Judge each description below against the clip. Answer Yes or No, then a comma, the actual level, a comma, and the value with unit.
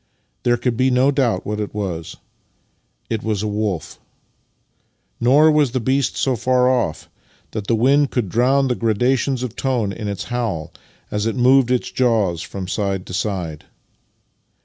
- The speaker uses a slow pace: No, average, 165 wpm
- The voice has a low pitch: Yes, low, 115 Hz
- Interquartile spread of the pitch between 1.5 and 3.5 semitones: No, average, 4.0 semitones